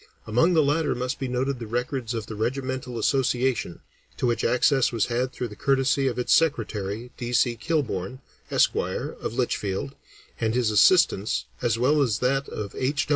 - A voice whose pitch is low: Yes, low, 125 Hz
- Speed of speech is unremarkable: Yes, average, 175 wpm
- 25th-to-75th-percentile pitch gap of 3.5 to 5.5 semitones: No, average, 3.1 semitones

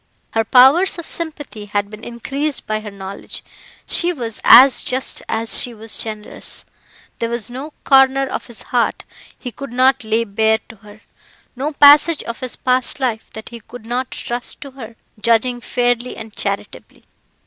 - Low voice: No, high, 240 Hz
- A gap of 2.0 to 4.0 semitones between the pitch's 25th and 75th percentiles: Yes, average, 3.3 semitones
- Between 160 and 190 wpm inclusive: Yes, average, 170 wpm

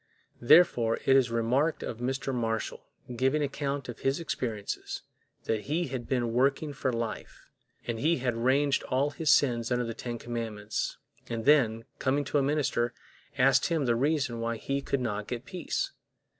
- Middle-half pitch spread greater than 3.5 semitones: No, average, 3.2 semitones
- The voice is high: No, low, 125 Hz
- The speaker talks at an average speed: Yes, average, 170 wpm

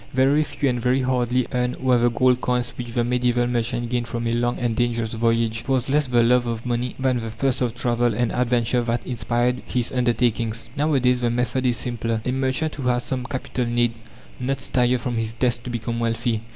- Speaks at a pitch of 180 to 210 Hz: No, low, 120 Hz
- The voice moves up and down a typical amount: No, narrow, 1.3 semitones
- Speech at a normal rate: No, fast, 215 wpm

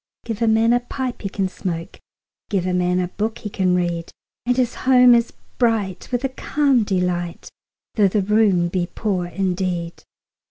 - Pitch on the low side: No, high, 195 Hz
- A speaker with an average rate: Yes, average, 185 wpm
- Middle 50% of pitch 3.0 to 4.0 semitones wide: No, average, 4.5 semitones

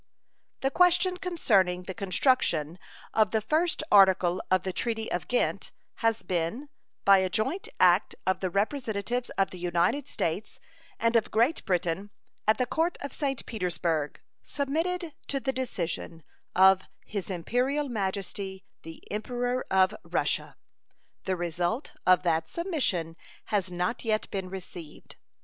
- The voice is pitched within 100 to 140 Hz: No, high, 200 Hz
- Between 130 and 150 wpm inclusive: Yes, average, 140 wpm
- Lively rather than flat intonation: Yes, wide, 6.0 semitones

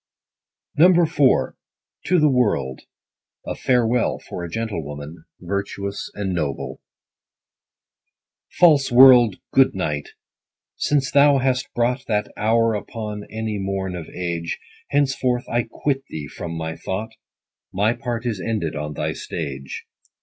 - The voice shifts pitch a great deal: Yes, wide, 6.6 semitones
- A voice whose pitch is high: No, low, 110 Hz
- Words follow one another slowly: Yes, slow, 130 wpm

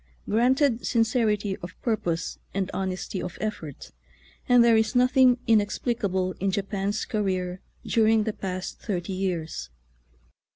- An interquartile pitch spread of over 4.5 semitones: No, average, 3.5 semitones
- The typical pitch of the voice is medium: No, high, 205 Hz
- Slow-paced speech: Yes, slow, 120 wpm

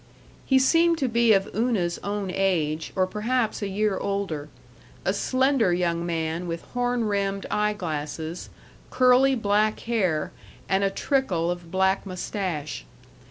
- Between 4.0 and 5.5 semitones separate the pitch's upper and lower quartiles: Yes, average, 4.9 semitones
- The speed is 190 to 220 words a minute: No, average, 140 wpm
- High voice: Yes, high, 195 Hz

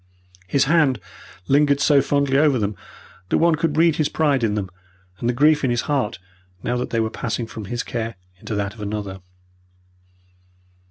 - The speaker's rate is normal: Yes, average, 180 wpm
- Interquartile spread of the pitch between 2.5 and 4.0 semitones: No, average, 4.8 semitones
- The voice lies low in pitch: Yes, low, 125 Hz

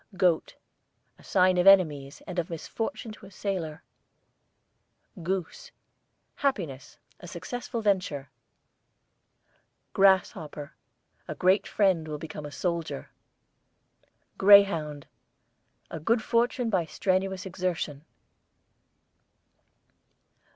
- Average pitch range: Yes, average, 3.9 semitones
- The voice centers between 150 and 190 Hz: Yes, medium, 185 Hz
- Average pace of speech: No, slow, 90 wpm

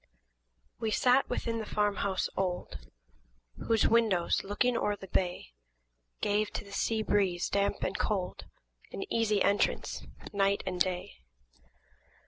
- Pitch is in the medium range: No, high, 205 Hz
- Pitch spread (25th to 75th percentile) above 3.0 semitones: No, average, 2.7 semitones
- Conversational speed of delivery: No, slow, 130 wpm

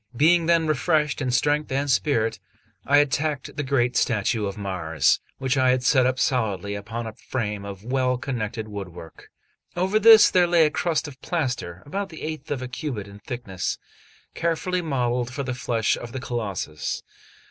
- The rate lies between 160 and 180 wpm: Yes, average, 175 wpm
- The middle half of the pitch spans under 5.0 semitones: No, wide, 5.6 semitones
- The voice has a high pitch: No, low, 130 Hz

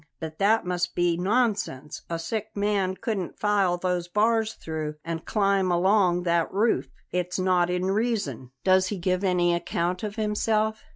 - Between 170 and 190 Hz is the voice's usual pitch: Yes, medium, 185 Hz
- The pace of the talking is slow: No, average, 160 wpm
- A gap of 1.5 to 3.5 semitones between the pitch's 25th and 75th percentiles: Yes, average, 3.1 semitones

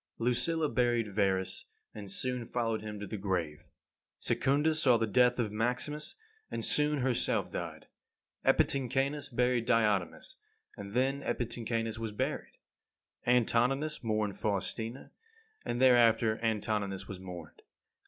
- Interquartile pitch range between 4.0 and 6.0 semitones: No, average, 3.2 semitones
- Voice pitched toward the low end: Yes, low, 115 Hz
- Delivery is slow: Yes, slow, 125 wpm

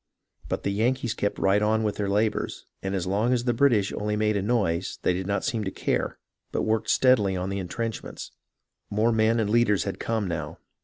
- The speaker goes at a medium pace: No, fast, 210 wpm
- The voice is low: Yes, low, 105 Hz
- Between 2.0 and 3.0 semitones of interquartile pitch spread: Yes, narrow, 2.6 semitones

